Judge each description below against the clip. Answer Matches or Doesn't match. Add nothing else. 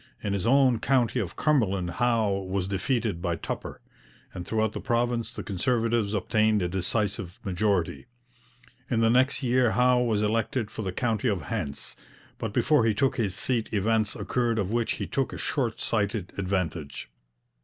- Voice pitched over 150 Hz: Doesn't match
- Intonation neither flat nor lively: Matches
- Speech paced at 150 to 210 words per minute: Matches